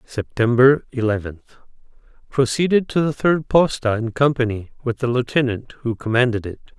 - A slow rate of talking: Yes, slow, 125 wpm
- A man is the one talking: Yes, male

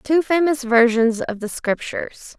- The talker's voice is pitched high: Yes, very high, 255 Hz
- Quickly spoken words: No, average, 150 wpm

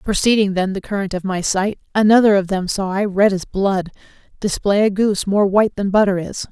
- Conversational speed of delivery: No, fast, 210 wpm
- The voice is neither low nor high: No, high, 200 Hz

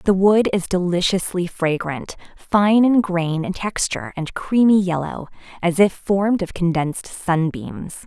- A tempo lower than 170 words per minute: Yes, average, 140 wpm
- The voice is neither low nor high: Yes, medium, 180 Hz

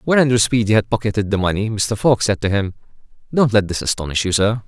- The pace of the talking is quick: Yes, fast, 230 wpm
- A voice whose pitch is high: No, low, 105 Hz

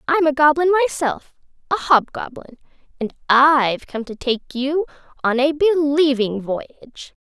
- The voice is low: No, very high, 280 Hz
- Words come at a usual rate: No, slow, 115 wpm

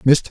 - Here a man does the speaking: Yes, male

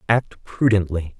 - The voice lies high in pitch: No, low, 100 Hz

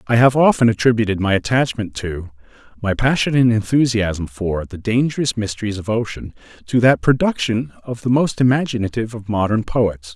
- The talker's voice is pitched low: Yes, low, 115 Hz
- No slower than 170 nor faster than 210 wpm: No, average, 155 wpm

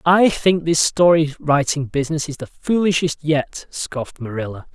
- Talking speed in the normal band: Yes, average, 150 wpm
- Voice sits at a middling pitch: Yes, medium, 155 Hz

